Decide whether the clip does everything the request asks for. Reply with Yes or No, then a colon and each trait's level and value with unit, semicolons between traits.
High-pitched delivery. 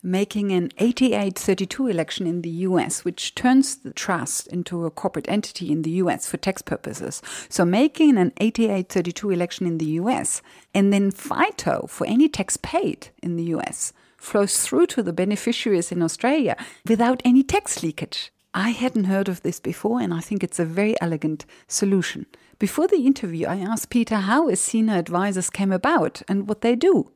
Yes: high, 195 Hz